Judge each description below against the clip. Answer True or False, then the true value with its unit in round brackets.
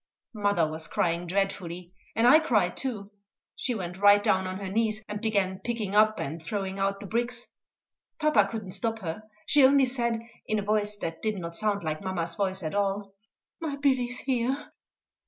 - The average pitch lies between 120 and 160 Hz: False (205 Hz)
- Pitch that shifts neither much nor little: True (3.7 semitones)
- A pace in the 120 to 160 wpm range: False (185 wpm)